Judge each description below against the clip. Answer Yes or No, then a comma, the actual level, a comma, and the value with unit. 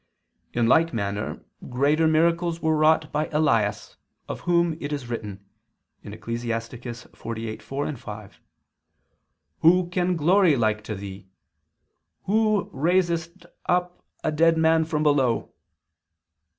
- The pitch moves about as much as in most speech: No, wide, 6.4 semitones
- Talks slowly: Yes, slow, 110 wpm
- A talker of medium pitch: Yes, medium, 150 Hz